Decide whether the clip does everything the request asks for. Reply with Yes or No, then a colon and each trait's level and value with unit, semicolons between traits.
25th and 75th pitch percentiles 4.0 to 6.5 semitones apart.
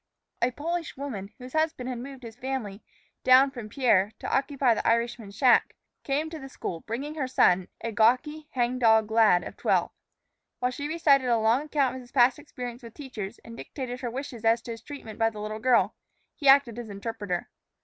No: average, 3.3 semitones